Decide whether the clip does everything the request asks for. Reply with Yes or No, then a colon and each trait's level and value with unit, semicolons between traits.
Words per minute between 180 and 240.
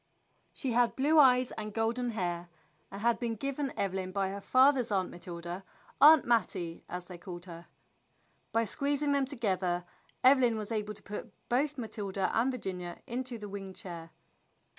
No: average, 170 wpm